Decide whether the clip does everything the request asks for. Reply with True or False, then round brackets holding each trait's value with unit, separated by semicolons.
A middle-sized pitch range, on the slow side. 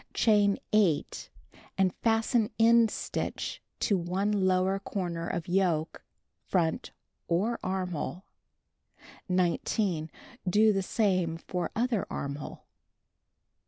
True (3.3 semitones; 95 wpm)